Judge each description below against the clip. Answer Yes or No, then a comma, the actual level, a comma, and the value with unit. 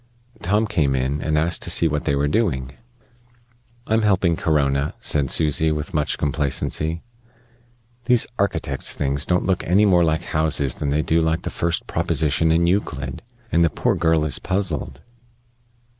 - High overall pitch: No, very low, 80 Hz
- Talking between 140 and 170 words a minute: Yes, average, 160 wpm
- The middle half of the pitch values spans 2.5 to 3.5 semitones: Yes, average, 3.0 semitones